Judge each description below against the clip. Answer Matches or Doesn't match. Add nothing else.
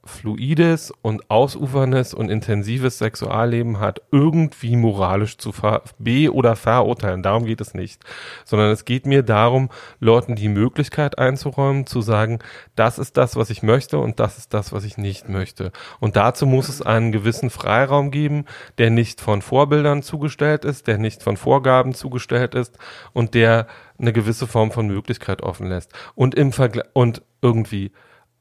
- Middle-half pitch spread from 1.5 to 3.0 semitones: Doesn't match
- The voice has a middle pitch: Doesn't match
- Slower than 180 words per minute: Matches